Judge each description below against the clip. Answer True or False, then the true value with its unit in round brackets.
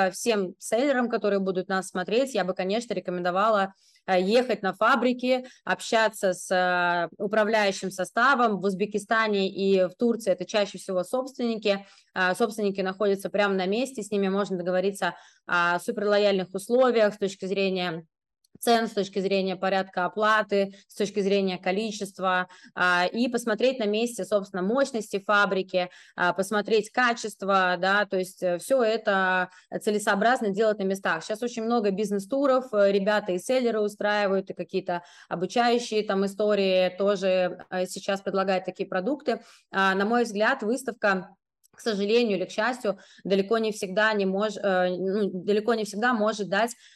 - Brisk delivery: False (135 wpm)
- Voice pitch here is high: True (200 Hz)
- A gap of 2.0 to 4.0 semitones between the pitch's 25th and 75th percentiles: True (2.8 semitones)